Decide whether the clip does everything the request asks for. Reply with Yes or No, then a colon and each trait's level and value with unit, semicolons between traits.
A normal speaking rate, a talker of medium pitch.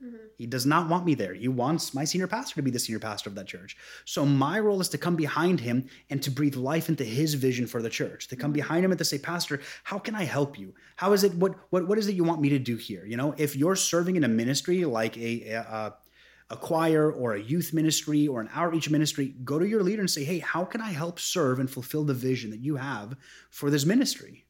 No: fast, 260 wpm; medium, 150 Hz